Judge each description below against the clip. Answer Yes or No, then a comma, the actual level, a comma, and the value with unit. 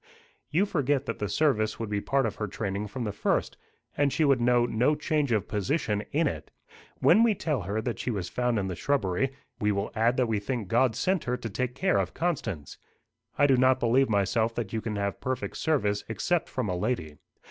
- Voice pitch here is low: Yes, low, 120 Hz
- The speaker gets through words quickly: Yes, fast, 220 wpm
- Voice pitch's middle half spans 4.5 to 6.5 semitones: Yes, average, 4.9 semitones